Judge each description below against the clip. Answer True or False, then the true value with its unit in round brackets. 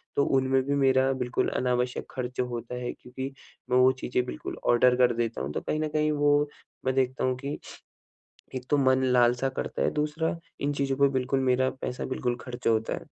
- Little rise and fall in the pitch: True (1.9 semitones)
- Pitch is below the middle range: True (130 Hz)